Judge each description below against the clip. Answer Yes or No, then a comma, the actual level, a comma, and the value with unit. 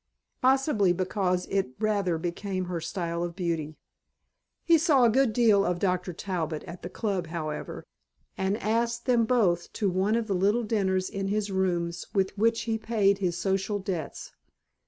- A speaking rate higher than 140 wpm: Yes, average, 165 wpm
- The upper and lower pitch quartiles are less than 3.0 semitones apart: No, average, 3.6 semitones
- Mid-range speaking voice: No, high, 195 Hz